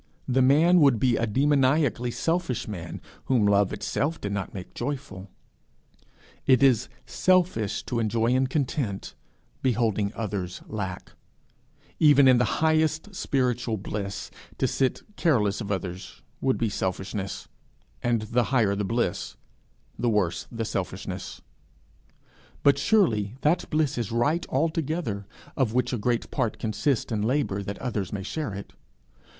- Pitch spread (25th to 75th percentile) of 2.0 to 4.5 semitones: No, average, 5.3 semitones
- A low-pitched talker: Yes, low, 120 Hz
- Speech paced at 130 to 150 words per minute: Yes, average, 140 wpm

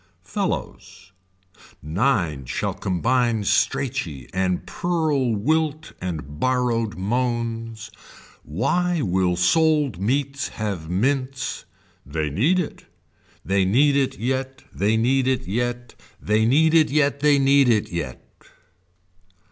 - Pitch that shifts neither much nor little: No, wide, 6.7 semitones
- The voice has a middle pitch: No, low, 120 Hz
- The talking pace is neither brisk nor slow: No, slow, 110 wpm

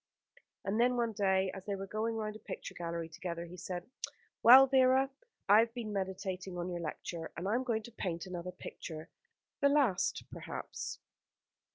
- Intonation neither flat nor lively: Yes, average, 4.4 semitones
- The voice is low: No, high, 195 Hz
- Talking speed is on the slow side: No, average, 180 wpm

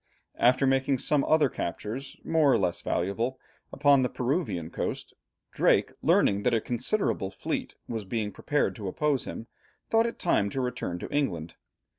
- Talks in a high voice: No, low, 125 Hz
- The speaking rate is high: No, average, 160 wpm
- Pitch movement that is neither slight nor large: No, wide, 5.9 semitones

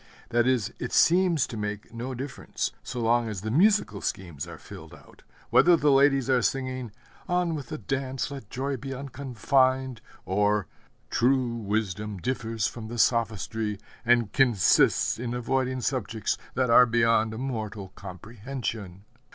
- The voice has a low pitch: Yes, low, 120 Hz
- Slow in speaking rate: No, average, 145 wpm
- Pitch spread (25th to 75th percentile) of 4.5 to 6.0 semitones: No, average, 3.6 semitones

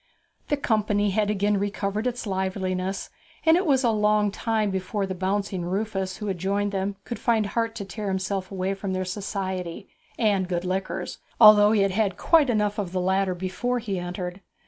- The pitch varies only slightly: Yes, narrow, 2.1 semitones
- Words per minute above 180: Yes, average, 190 wpm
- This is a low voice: No, high, 200 Hz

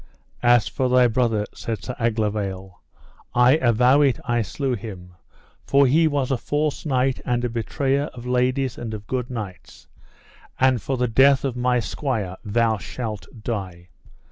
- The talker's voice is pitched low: Yes, low, 120 Hz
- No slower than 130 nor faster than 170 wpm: Yes, average, 160 wpm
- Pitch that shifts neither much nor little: Yes, average, 3.3 semitones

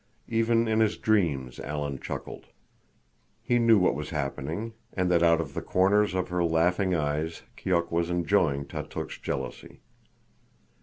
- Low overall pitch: Yes, very low, 85 Hz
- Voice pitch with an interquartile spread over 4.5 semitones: Yes, average, 5.2 semitones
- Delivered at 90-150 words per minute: Yes, average, 145 wpm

